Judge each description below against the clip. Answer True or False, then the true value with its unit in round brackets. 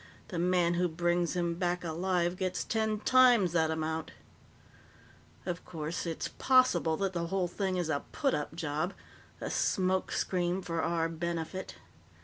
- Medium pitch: True (175 Hz)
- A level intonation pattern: True (2.1 semitones)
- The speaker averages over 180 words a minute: False (150 wpm)